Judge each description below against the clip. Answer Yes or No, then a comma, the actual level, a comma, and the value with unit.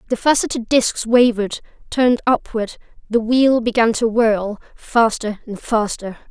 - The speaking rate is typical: No, slow, 105 wpm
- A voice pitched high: Yes, high, 230 Hz